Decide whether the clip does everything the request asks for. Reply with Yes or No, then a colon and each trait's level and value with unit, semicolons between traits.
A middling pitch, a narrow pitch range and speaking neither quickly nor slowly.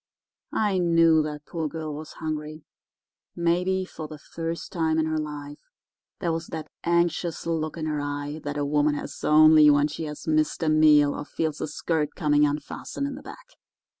Yes: medium, 155 Hz; narrow, 1.8 semitones; average, 180 wpm